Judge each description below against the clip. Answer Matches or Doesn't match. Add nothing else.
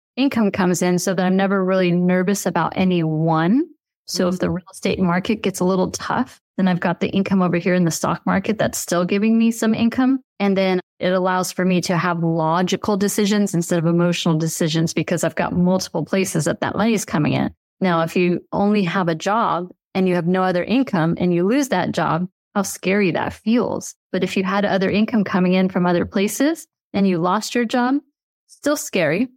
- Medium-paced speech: Doesn't match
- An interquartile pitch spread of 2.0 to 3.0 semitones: Matches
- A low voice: Doesn't match